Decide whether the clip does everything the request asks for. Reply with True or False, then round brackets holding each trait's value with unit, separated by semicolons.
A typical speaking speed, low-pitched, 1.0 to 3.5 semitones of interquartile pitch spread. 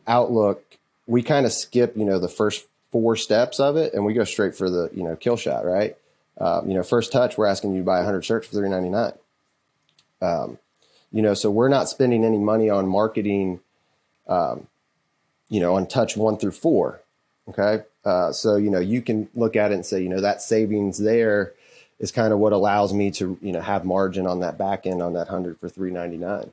False (215 wpm; 100 Hz; 2.9 semitones)